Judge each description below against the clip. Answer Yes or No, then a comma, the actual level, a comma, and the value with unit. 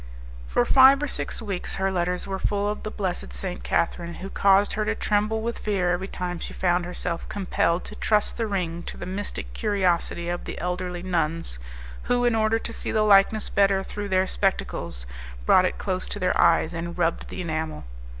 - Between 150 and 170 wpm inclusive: No, average, 200 wpm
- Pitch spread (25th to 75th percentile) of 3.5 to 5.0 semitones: No, average, 3.0 semitones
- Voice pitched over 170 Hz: Yes, medium, 185 Hz